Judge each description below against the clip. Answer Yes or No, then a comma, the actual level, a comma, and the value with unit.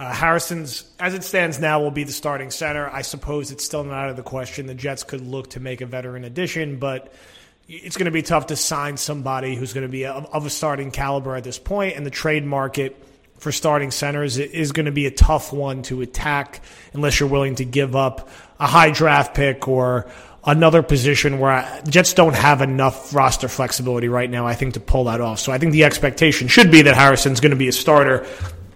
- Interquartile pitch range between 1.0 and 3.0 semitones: Yes, narrow, 2.5 semitones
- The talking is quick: Yes, fast, 225 wpm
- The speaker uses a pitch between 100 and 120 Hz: No, medium, 140 Hz